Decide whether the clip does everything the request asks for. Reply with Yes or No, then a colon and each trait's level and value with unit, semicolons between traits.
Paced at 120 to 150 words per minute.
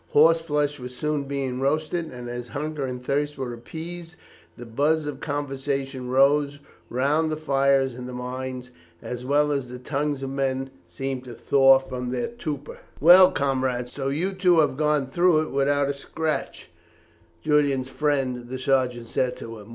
No: average, 170 wpm